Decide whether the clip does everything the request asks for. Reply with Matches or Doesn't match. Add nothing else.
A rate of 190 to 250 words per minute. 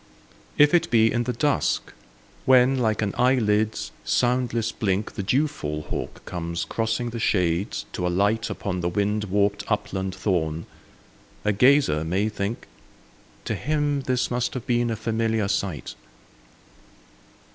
Doesn't match